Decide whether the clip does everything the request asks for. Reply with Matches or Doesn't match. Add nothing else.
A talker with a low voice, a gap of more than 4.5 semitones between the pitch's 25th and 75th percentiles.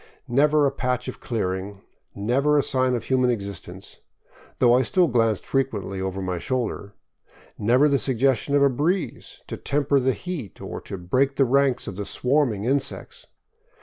Matches